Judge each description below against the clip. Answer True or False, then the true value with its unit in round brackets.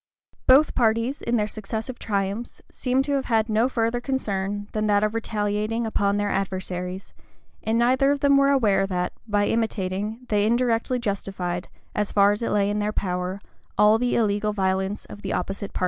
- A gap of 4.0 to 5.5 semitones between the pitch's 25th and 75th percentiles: False (2.9 semitones)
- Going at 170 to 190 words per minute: True (180 wpm)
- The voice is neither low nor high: False (210 Hz)